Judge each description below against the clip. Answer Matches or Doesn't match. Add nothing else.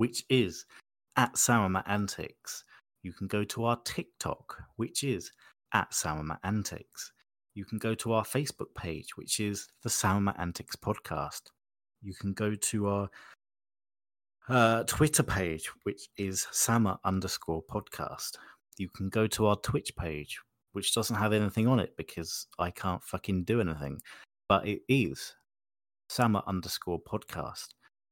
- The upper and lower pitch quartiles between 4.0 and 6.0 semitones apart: Doesn't match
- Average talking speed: Matches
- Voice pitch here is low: Matches